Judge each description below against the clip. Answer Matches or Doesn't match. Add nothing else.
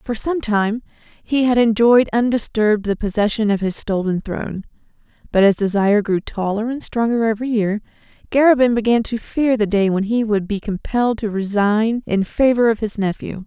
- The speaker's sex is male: Doesn't match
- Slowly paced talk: Doesn't match